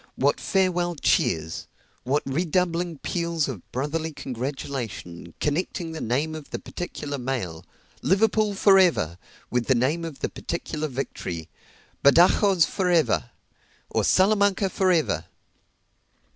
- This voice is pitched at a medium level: Yes, medium, 155 Hz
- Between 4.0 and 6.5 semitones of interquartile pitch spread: Yes, wide, 5.5 semitones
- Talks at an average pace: No, slow, 120 wpm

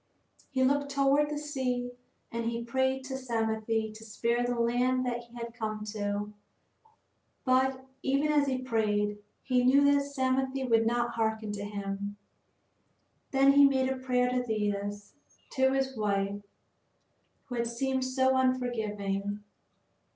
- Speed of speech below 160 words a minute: Yes, average, 145 wpm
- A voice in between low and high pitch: No, high, 245 Hz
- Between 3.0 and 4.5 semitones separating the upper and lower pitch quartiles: Yes, average, 3.3 semitones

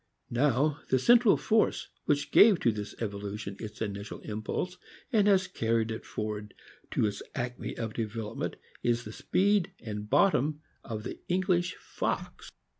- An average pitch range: No, wide, 8.8 semitones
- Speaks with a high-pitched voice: No, low, 120 Hz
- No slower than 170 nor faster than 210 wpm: No, average, 150 wpm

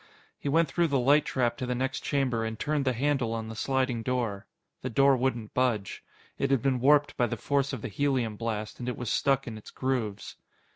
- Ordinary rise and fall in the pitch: Yes, average, 3.2 semitones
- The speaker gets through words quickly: Yes, fast, 225 wpm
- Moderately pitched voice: No, low, 125 Hz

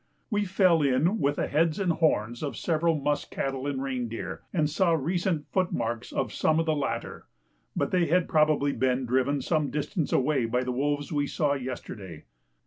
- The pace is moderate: Yes, average, 180 wpm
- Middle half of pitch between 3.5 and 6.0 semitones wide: Yes, average, 3.9 semitones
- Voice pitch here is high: No, medium, 145 Hz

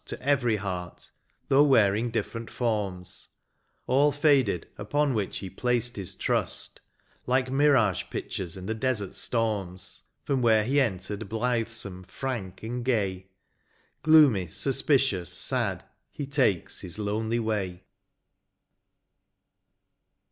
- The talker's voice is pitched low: Yes, low, 110 Hz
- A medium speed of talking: No, slow, 110 wpm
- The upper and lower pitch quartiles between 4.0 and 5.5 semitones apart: Yes, average, 5.0 semitones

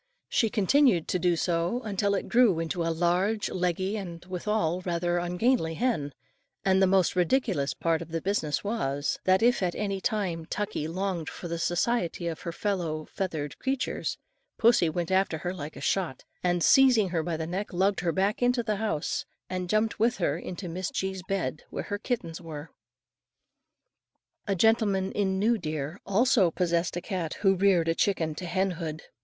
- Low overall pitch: No, medium, 185 Hz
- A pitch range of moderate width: Yes, average, 3.5 semitones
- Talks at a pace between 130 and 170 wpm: No, average, 180 wpm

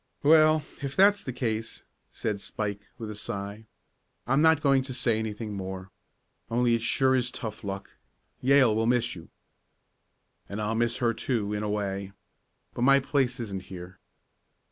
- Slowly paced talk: No, average, 165 wpm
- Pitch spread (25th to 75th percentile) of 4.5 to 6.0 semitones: No, average, 4.1 semitones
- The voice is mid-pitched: No, low, 115 Hz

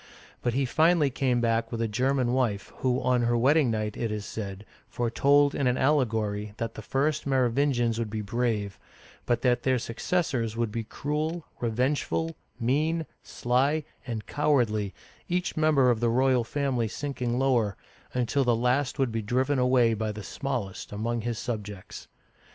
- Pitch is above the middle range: No, low, 120 Hz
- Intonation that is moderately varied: Yes, average, 3.3 semitones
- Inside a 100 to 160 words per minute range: No, average, 170 wpm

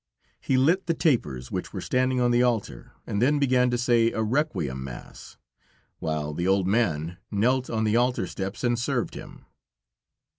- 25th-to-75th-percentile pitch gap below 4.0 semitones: No, average, 5.2 semitones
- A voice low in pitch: Yes, low, 120 Hz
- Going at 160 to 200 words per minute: Yes, average, 175 wpm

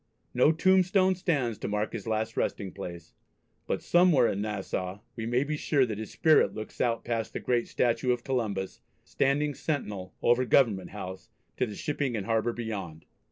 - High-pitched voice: No, low, 115 Hz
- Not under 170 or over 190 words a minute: Yes, average, 175 wpm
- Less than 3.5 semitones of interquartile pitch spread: No, average, 4.9 semitones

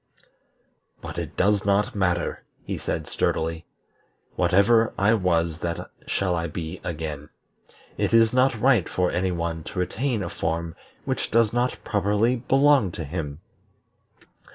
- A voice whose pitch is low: Yes, very low, 95 Hz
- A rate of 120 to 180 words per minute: Yes, average, 140 wpm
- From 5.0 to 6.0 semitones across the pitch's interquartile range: Yes, average, 5.3 semitones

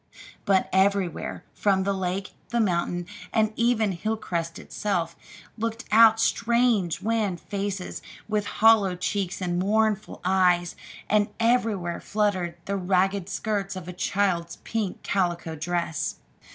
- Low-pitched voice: No, high, 195 Hz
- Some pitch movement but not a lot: Yes, average, 3.3 semitones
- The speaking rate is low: Yes, slow, 125 wpm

